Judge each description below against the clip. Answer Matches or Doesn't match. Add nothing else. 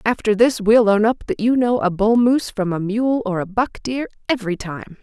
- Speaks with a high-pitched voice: Matches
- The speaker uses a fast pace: Matches